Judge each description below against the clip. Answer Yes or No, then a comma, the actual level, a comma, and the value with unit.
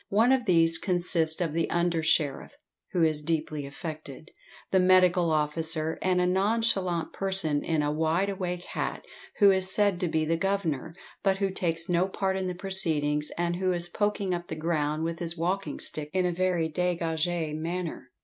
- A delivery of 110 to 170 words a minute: No, average, 180 wpm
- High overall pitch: No, medium, 175 Hz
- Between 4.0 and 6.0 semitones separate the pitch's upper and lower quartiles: No, average, 2.8 semitones